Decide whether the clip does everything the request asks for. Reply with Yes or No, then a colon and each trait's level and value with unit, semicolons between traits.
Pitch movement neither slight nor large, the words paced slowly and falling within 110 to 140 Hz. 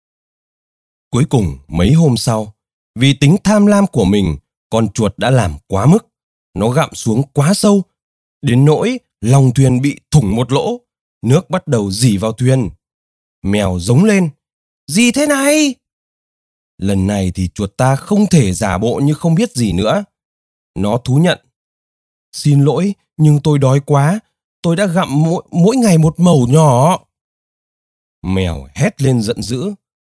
No: wide, 8.6 semitones; slow, 155 wpm; low, 135 Hz